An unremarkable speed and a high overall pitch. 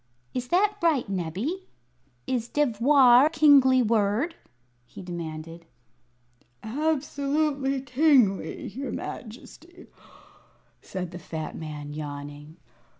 No: slow, 90 wpm; high, 245 Hz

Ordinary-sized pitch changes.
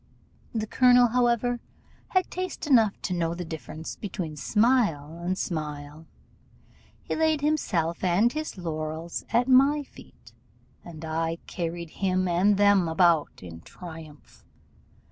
No: wide, 6.8 semitones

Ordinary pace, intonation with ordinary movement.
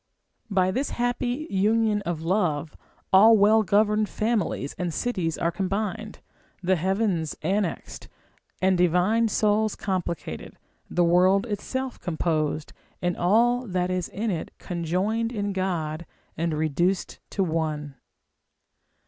No: slow, 120 wpm; average, 4.1 semitones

